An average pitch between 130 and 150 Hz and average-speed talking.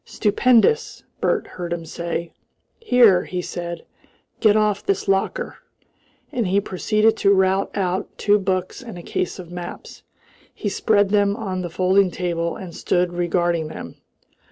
No: high, 190 Hz; average, 150 wpm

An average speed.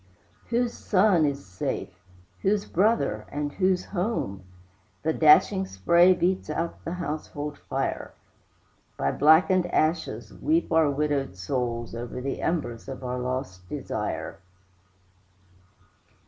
No: slow, 115 wpm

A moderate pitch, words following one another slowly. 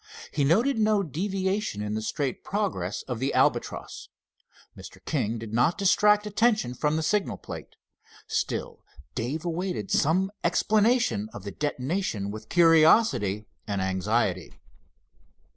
Yes: medium, 155 Hz; slow, 125 wpm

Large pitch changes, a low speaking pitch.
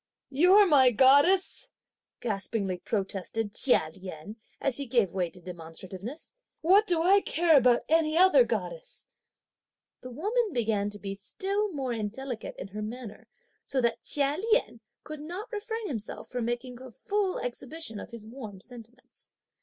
No: wide, 8.0 semitones; very high, 255 Hz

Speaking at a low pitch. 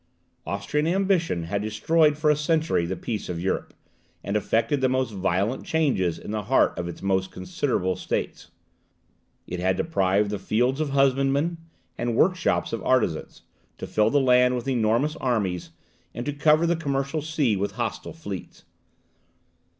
Yes: low, 125 Hz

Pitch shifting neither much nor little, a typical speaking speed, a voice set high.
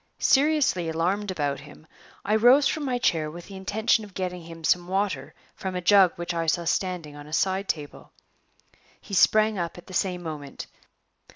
No: average, 3.8 semitones; average, 185 wpm; medium, 180 Hz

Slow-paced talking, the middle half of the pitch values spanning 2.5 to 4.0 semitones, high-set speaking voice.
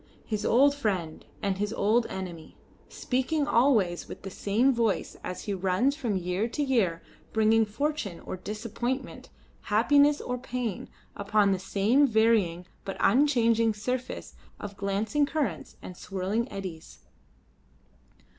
No: slow, 130 wpm; average, 4.4 semitones; high, 220 Hz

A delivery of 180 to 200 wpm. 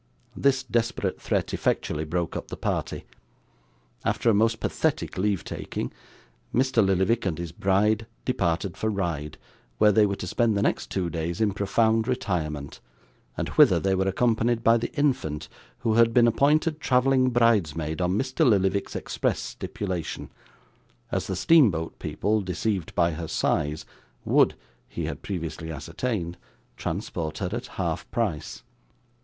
No: average, 145 wpm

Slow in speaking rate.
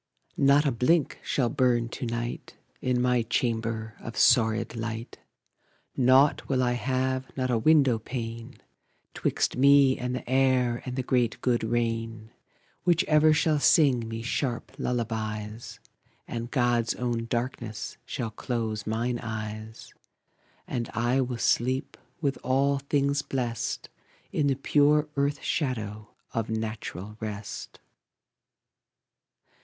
Yes: slow, 125 wpm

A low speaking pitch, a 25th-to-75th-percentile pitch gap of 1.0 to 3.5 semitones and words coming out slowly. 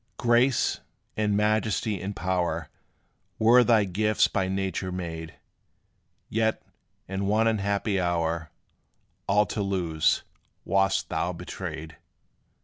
Yes: low, 100 Hz; average, 3.0 semitones; slow, 105 wpm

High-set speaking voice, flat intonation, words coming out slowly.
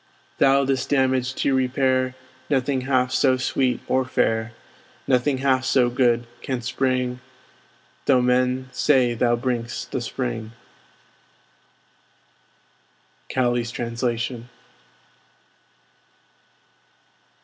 No: low, 130 Hz; narrow, 1.4 semitones; slow, 90 wpm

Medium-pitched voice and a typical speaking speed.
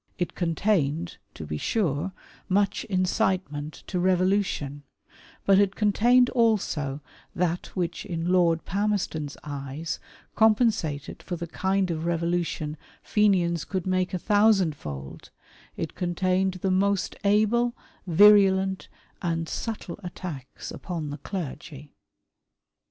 No: medium, 180 Hz; slow, 120 wpm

